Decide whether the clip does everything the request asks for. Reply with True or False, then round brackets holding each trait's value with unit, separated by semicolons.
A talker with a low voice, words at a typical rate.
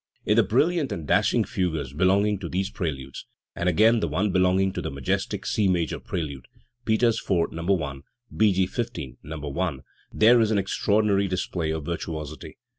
True (95 Hz; 175 wpm)